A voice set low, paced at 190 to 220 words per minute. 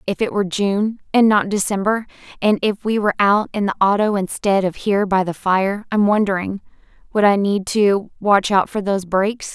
No: high, 200 Hz; average, 195 wpm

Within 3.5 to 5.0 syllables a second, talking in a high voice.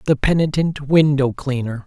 No: 4.7 syllables/s; medium, 140 Hz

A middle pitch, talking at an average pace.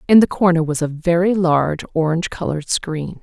Yes: medium, 165 Hz; average, 185 wpm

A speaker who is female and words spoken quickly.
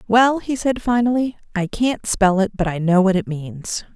Yes: female; fast, 210 wpm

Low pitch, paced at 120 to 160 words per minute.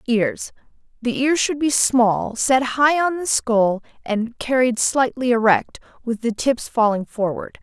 No: high, 200 Hz; average, 150 wpm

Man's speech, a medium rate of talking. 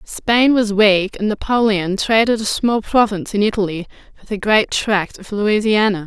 No: female; average, 170 wpm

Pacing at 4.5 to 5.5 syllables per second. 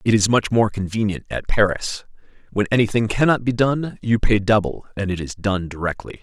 Yes: 5.3 syllables/s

